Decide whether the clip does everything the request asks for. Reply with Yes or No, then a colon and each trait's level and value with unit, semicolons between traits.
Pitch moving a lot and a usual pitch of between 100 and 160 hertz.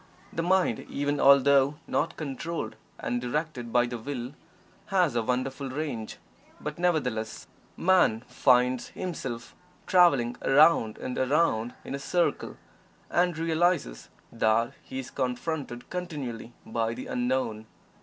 No: average, 4.9 semitones; low, 135 Hz